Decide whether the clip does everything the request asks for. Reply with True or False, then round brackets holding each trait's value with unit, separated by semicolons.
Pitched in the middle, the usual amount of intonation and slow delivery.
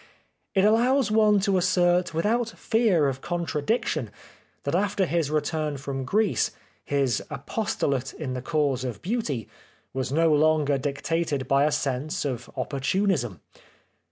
False (155 Hz; 5.9 semitones; 130 wpm)